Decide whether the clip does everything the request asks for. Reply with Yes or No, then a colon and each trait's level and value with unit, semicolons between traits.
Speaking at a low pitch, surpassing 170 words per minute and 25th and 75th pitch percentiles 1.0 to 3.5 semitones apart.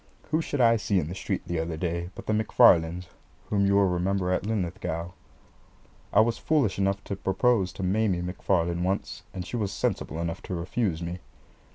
Yes: very low, 95 Hz; average, 190 wpm; average, 2.9 semitones